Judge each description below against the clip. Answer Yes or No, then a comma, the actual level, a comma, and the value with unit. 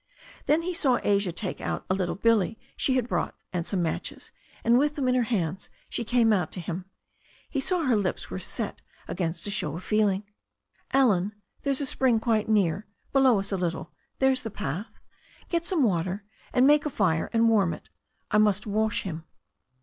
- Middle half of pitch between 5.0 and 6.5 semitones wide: Yes, wide, 5.4 semitones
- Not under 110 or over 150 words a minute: No, average, 195 wpm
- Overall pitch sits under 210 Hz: No, high, 215 Hz